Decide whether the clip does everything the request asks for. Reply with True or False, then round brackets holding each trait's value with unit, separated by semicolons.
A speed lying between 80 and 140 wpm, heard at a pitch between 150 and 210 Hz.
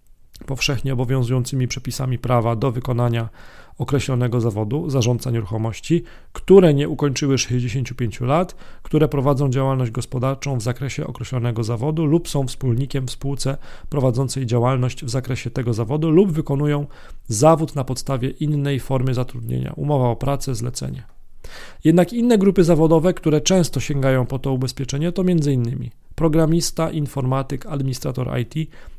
False (130 wpm; 135 Hz)